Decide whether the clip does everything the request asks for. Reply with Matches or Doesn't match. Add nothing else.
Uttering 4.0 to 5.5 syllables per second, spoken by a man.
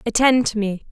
Doesn't match